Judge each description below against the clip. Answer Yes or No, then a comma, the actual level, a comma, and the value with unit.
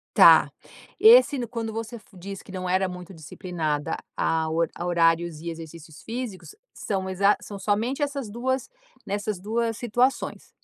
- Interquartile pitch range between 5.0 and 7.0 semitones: Yes, average, 5.3 semitones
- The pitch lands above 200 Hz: No, high, 195 Hz